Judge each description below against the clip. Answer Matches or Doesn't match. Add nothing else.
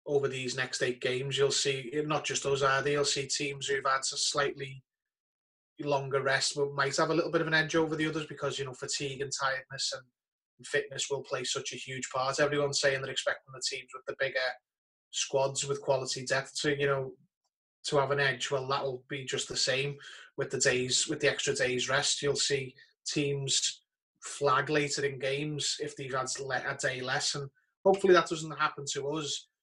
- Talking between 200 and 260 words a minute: Matches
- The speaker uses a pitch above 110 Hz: Matches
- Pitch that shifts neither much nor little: Doesn't match